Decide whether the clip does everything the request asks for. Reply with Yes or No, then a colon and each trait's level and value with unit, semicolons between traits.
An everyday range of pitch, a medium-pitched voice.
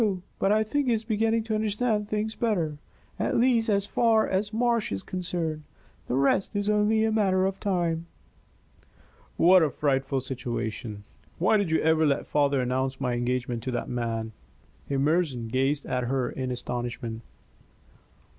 No: wide, 8.7 semitones; medium, 160 Hz